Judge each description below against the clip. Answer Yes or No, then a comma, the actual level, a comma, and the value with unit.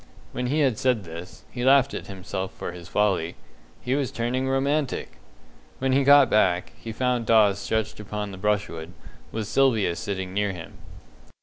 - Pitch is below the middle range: Yes, low, 110 Hz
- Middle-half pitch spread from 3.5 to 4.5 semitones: No, average, 5.3 semitones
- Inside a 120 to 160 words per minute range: No, average, 170 wpm